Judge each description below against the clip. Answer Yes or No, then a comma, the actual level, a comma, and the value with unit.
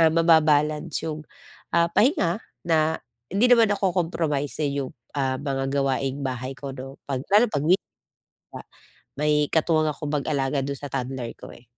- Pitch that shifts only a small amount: No, average, 3.4 semitones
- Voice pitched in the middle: Yes, medium, 150 Hz